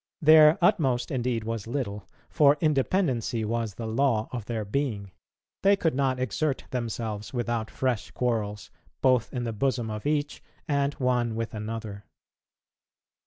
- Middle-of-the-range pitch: No, low, 120 Hz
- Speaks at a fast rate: No, average, 140 wpm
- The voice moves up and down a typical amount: Yes, average, 4.0 semitones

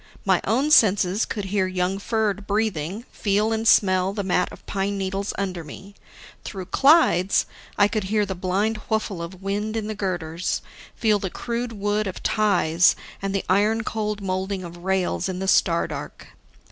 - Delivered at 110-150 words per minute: No, average, 170 wpm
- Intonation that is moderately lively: No, narrow, 2.3 semitones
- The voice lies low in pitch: No, high, 195 Hz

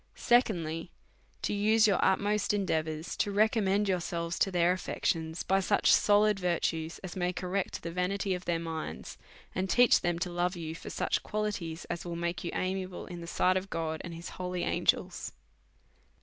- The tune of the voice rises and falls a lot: No, average, 2.7 semitones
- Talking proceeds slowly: No, average, 180 wpm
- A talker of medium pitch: Yes, medium, 180 Hz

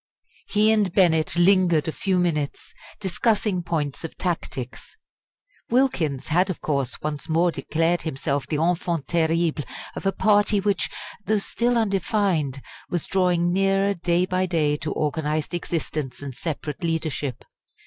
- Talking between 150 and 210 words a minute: No, average, 140 wpm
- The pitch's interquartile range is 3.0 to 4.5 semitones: Yes, average, 3.9 semitones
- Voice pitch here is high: No, medium, 170 Hz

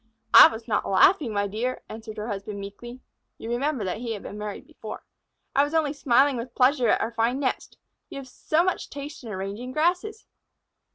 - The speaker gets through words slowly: No, average, 195 wpm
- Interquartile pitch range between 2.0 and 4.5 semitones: No, average, 4.9 semitones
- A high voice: Yes, high, 240 Hz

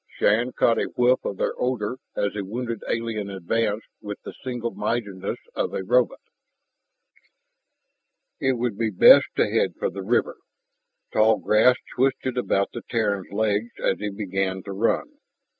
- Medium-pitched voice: No, low, 110 Hz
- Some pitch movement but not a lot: Yes, average, 3.2 semitones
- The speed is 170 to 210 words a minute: No, average, 155 wpm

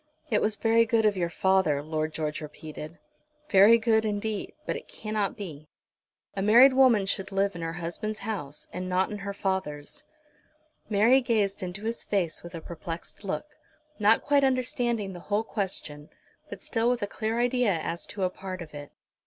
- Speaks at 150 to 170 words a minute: No, average, 180 wpm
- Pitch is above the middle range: Yes, high, 200 Hz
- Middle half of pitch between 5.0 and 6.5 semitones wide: No, average, 4.5 semitones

